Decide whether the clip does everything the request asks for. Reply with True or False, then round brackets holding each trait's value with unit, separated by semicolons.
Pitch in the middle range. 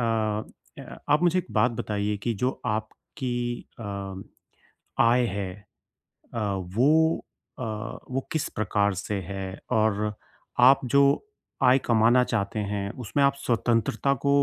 False (115 Hz)